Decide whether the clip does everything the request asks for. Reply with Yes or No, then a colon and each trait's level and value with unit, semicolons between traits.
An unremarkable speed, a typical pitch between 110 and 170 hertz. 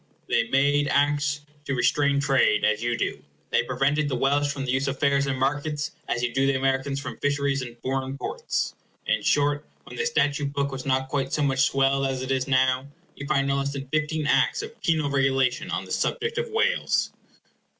No: fast, 210 wpm; medium, 140 Hz